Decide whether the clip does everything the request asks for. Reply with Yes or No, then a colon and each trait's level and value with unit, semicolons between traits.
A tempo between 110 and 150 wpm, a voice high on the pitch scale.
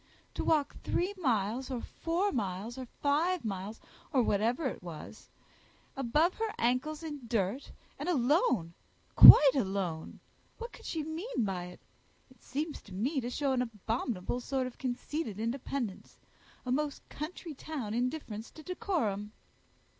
Yes: average, 145 wpm; very high, 255 Hz